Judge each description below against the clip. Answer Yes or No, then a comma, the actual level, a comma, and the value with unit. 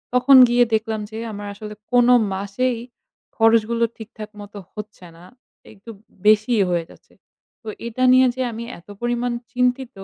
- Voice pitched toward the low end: No, high, 225 Hz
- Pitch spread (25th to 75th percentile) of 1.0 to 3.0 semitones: Yes, average, 2.7 semitones